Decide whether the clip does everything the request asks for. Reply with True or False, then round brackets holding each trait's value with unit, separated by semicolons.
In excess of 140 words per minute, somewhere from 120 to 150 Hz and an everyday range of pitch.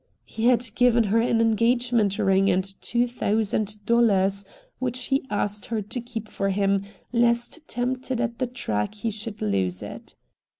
False (160 wpm; 225 Hz; 3.3 semitones)